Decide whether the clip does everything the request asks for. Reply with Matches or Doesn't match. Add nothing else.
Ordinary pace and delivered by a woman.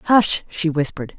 Matches